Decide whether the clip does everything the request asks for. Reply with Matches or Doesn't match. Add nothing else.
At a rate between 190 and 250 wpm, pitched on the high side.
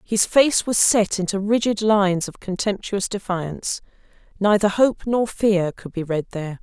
Doesn't match